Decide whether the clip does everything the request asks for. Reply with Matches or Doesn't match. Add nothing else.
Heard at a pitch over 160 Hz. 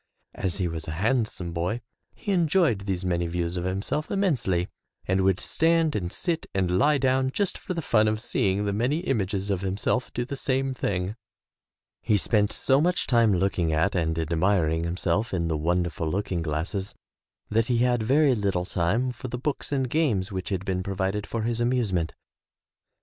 Doesn't match